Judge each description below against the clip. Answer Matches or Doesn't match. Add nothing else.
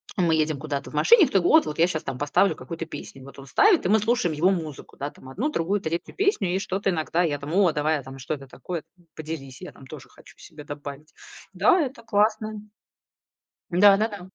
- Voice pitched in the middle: Matches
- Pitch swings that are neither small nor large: Doesn't match